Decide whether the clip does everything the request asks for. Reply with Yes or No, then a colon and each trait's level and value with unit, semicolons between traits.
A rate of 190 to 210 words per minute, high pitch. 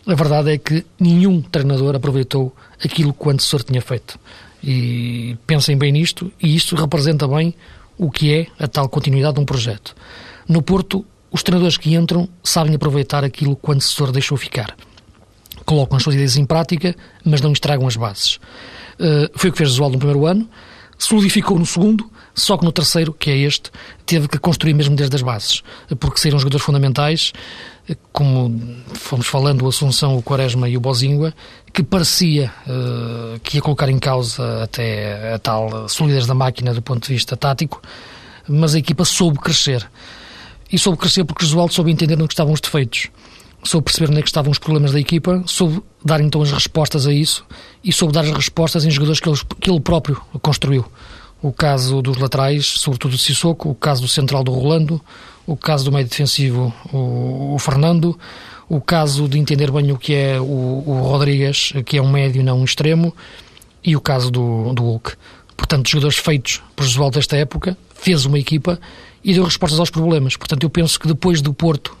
No: fast, 195 wpm; medium, 145 Hz